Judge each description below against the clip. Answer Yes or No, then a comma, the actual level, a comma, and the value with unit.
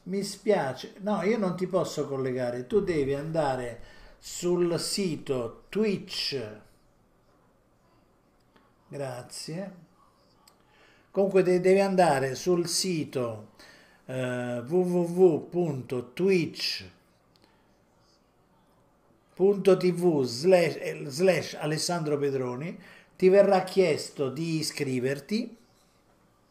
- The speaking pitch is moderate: Yes, medium, 175 Hz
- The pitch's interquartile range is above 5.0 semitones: Yes, wide, 5.5 semitones